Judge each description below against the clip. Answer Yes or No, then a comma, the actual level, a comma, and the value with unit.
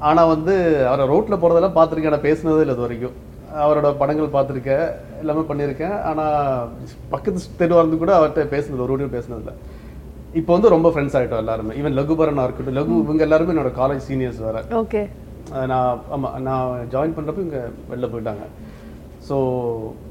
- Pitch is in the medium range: Yes, medium, 145 Hz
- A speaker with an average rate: No, fast, 160 wpm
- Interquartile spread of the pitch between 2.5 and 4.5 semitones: Yes, average, 4.0 semitones